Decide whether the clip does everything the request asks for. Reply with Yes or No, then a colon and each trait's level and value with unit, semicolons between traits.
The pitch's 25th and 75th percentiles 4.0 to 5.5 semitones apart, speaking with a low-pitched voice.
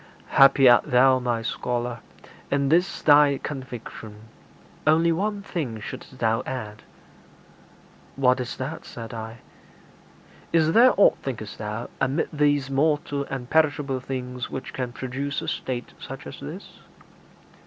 No: average, 3.3 semitones; low, 130 Hz